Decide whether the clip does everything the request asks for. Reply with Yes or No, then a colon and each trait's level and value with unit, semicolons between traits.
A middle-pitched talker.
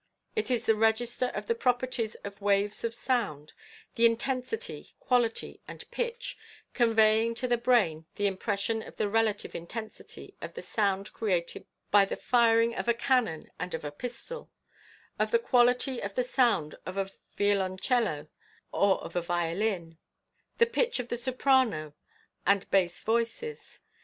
No: high, 225 Hz